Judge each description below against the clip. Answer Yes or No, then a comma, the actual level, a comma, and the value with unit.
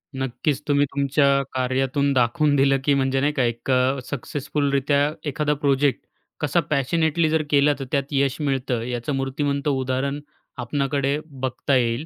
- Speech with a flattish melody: Yes, narrow, 1.7 semitones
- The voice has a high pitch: No, medium, 140 Hz